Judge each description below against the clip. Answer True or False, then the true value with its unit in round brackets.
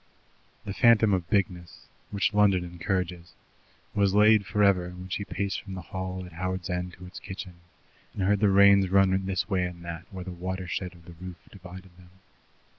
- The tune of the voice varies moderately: False (1.8 semitones)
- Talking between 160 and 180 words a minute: False (190 wpm)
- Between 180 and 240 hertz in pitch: False (95 Hz)